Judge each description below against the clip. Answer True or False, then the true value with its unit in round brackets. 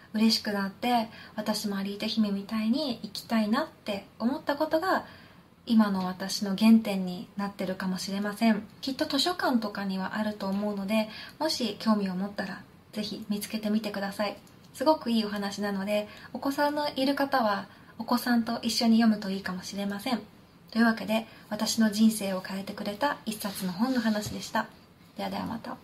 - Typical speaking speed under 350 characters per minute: False (360 characters per minute)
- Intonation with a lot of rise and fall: False (2.6 semitones)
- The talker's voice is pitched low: False (215 Hz)